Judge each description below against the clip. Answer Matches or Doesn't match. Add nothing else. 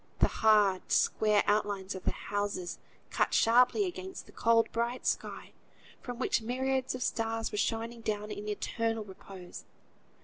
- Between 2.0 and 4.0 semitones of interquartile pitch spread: Matches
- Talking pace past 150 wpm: Doesn't match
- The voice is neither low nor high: Doesn't match